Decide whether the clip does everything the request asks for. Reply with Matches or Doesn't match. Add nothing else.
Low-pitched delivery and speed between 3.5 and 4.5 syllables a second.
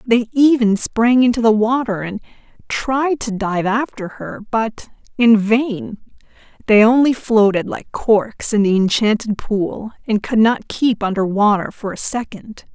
Doesn't match